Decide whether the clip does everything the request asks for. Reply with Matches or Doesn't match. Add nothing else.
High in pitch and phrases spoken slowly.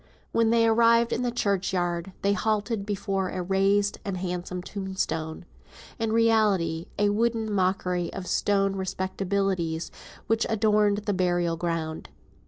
Matches